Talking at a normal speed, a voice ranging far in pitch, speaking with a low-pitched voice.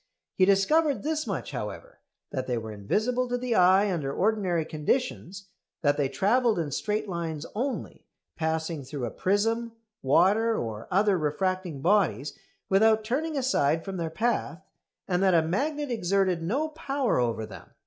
No: average, 155 wpm; wide, 6.5 semitones; high, 190 Hz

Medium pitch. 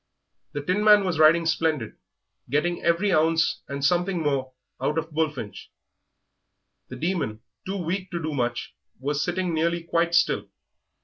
Yes: medium, 165 Hz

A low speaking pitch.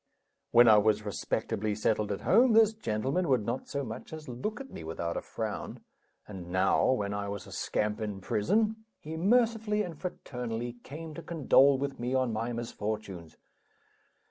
Yes: low, 120 Hz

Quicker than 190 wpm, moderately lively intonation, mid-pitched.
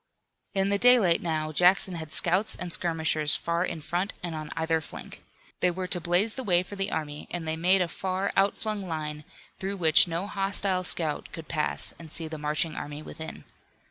Yes: average, 200 wpm; average, 3.2 semitones; medium, 175 Hz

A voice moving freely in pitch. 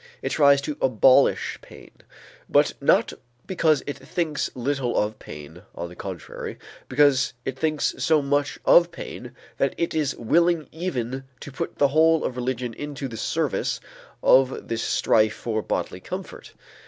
No: average, 3.9 semitones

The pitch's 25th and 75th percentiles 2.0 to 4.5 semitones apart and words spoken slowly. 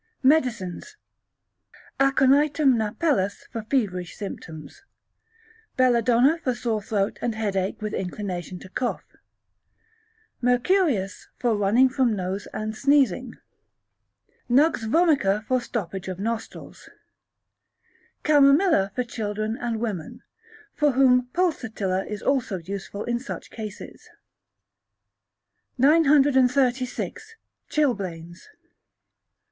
No: average, 5.2 semitones; slow, 90 wpm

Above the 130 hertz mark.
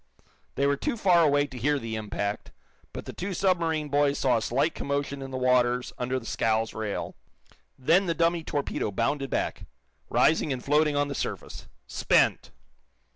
Yes: medium, 140 Hz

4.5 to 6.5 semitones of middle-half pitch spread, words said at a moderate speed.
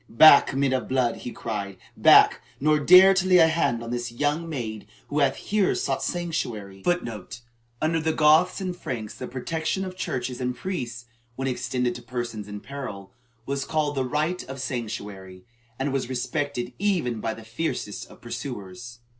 Yes: average, 5.1 semitones; average, 170 wpm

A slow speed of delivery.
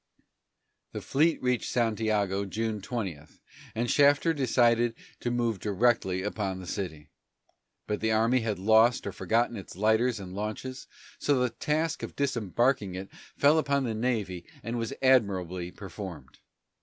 No: average, 145 wpm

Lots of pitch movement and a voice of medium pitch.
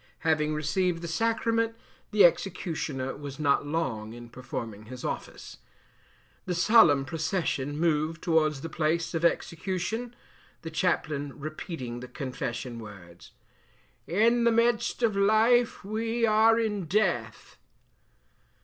Yes: wide, 7.3 semitones; medium, 165 Hz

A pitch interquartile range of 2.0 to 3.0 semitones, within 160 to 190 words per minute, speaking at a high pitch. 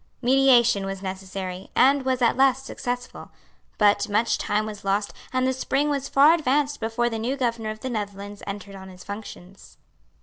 No: average, 4.5 semitones; average, 175 wpm; high, 225 Hz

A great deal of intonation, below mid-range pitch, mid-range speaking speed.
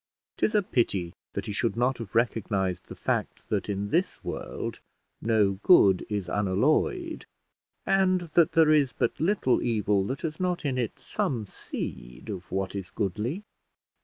Yes: wide, 7.9 semitones; low, 115 Hz; average, 160 wpm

